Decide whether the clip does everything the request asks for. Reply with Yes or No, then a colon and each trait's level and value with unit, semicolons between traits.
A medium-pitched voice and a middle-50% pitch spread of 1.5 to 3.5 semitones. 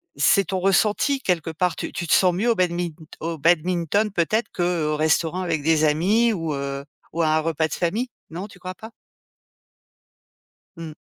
Yes: medium, 175 Hz; average, 3.2 semitones